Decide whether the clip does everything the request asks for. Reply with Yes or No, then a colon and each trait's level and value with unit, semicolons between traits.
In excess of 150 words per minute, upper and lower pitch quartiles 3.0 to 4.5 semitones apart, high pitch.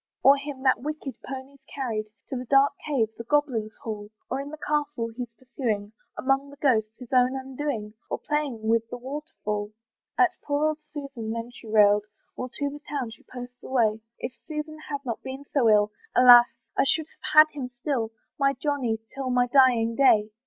Yes: average, 190 wpm; average, 3.8 semitones; very high, 260 Hz